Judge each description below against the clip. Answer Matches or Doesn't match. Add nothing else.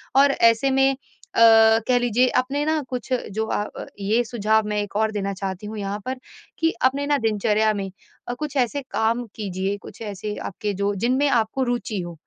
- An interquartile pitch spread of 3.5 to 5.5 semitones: Matches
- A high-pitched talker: Matches